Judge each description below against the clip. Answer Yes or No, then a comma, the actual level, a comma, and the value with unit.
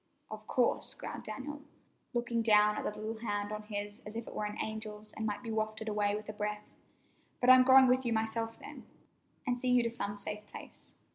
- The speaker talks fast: Yes, fast, 215 wpm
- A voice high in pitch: Yes, high, 220 Hz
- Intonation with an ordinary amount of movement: No, narrow, 2.0 semitones